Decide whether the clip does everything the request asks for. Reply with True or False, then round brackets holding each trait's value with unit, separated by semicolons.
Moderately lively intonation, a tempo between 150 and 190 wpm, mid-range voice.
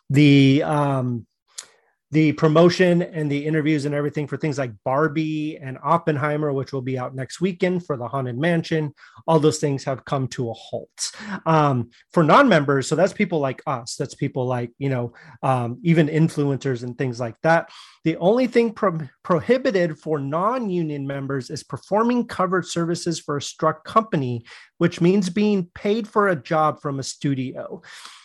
True (3.9 semitones; 170 wpm; 155 Hz)